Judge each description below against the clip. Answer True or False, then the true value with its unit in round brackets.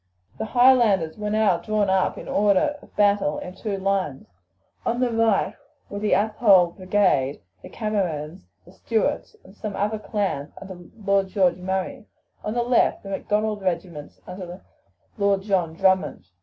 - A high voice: True (195 Hz)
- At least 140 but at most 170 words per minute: True (155 wpm)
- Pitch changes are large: False (2.6 semitones)